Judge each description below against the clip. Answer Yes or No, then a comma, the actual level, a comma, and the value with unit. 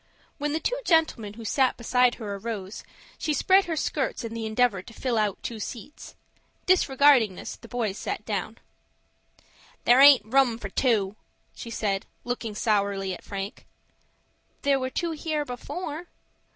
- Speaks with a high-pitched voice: Yes, high, 235 Hz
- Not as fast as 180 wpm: Yes, average, 150 wpm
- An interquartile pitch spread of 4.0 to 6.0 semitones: Yes, average, 5.1 semitones